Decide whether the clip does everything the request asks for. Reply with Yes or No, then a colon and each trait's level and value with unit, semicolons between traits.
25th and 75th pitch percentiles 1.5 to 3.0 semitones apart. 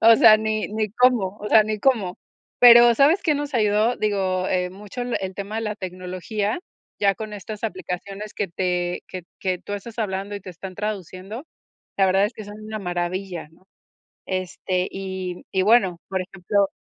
Yes: average, 2.7 semitones